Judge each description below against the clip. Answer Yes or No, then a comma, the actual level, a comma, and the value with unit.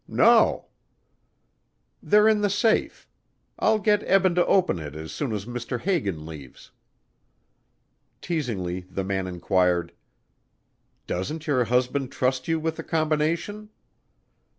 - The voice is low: Yes, low, 130 Hz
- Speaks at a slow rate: Yes, slow, 120 wpm